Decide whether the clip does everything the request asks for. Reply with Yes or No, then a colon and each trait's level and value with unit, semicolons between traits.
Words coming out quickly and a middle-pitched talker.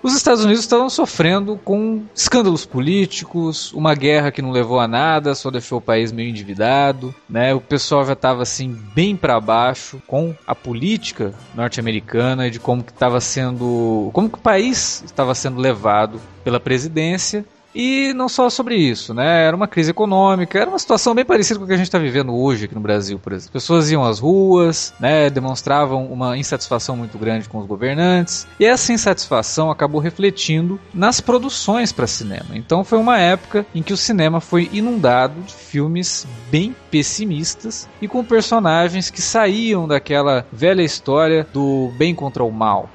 No: average, 175 wpm; medium, 155 Hz